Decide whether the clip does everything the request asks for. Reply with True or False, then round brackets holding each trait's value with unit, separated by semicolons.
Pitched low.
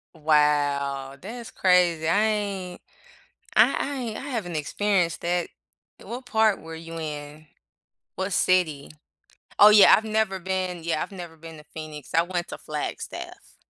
False (175 Hz)